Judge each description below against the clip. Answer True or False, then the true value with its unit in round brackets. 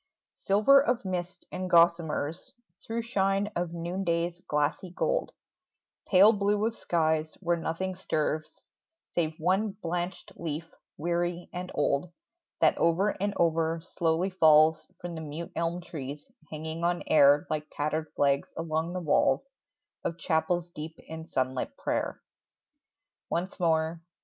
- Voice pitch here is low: False (170 Hz)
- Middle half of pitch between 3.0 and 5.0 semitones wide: False (2.5 semitones)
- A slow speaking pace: True (130 wpm)